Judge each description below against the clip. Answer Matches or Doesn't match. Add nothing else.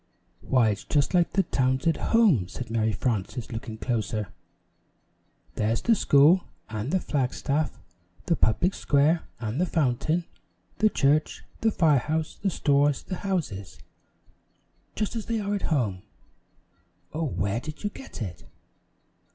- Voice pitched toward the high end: Doesn't match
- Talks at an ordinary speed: Matches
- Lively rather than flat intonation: Matches